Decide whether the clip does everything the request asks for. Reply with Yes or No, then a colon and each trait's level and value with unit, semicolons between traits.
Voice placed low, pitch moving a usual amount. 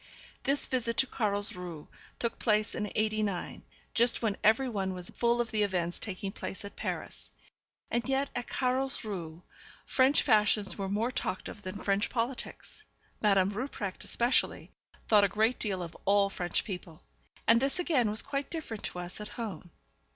No: high, 210 Hz; average, 3.7 semitones